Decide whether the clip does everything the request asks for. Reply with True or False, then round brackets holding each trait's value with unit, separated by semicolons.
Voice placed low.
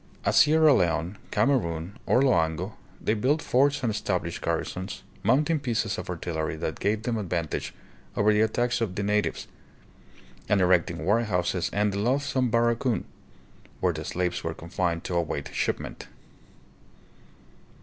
True (105 Hz)